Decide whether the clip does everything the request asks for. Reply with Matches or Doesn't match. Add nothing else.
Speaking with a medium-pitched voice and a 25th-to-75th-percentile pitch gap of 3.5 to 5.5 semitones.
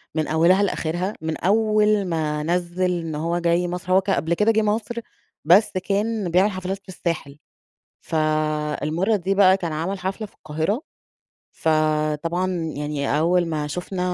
Matches